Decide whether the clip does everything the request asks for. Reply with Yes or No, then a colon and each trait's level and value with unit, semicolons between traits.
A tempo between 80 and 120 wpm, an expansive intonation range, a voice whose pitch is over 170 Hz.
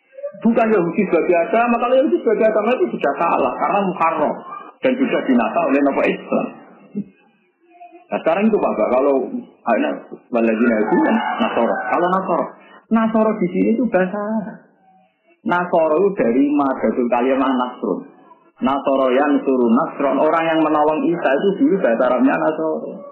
No: fast, 140 wpm; wide, 7.2 semitones; high, 190 Hz